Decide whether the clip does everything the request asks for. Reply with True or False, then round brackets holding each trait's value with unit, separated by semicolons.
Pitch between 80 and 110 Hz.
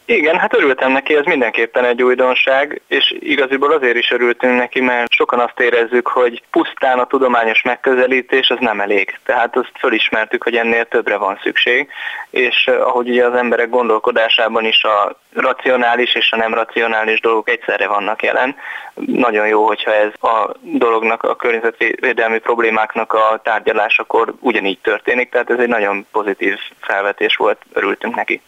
False (125 Hz)